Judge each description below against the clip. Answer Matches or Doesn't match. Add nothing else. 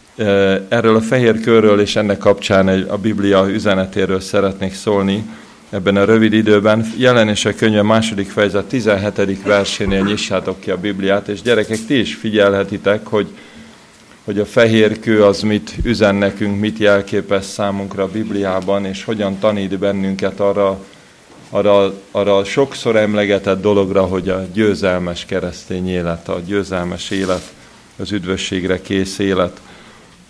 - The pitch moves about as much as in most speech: Doesn't match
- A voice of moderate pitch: Doesn't match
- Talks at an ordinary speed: Matches